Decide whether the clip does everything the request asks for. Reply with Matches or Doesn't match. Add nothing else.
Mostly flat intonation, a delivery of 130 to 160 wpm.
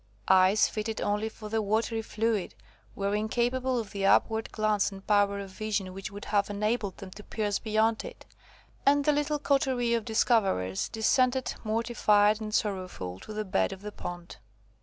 Doesn't match